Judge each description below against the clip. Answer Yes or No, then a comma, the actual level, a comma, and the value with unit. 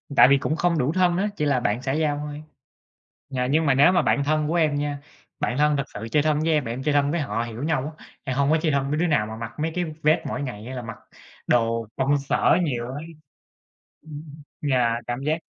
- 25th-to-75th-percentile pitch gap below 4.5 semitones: Yes, average, 3.4 semitones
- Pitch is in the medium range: Yes, medium, 145 Hz